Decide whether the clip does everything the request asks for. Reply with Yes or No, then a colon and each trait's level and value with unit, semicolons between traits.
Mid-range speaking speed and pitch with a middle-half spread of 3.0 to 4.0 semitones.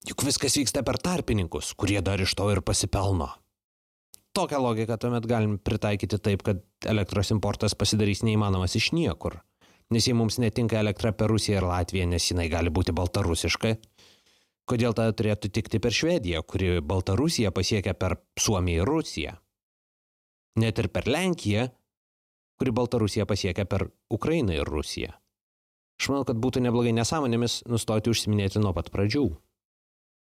Yes: average, 145 wpm; average, 3.7 semitones